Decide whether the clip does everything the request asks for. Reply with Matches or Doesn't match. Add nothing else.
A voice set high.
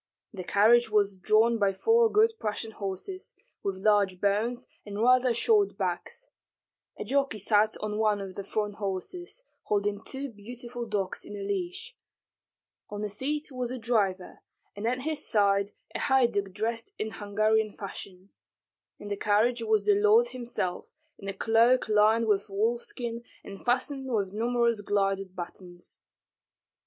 Matches